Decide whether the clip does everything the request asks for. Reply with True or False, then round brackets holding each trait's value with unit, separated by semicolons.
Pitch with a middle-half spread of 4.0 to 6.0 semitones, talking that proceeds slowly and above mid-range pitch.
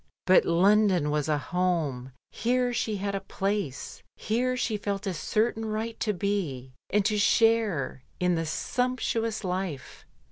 False (4.7 semitones; 150 wpm; 200 Hz)